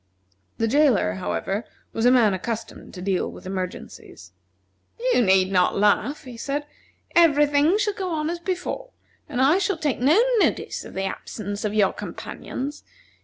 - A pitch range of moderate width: No, wide, 7.8 semitones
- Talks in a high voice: Yes, very high, 255 Hz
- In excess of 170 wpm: No, average, 165 wpm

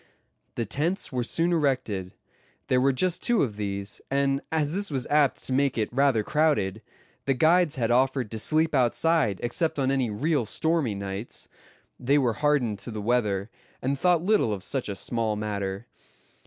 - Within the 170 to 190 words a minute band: Yes, average, 175 wpm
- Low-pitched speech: Yes, low, 130 Hz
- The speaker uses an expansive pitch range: Yes, wide, 5.7 semitones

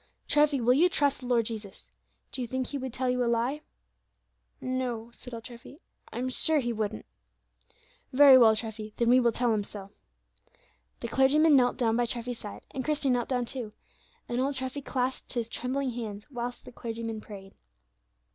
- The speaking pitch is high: Yes, high, 245 Hz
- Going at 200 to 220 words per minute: No, average, 185 wpm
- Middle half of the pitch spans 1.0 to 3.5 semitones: Yes, narrow, 2.4 semitones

